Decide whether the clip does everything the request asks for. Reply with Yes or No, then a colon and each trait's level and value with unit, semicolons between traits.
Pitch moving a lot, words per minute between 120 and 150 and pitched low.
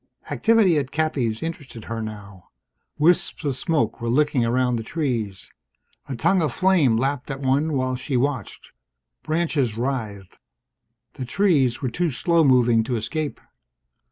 No: average, 4.9 semitones; average, 145 wpm; low, 130 Hz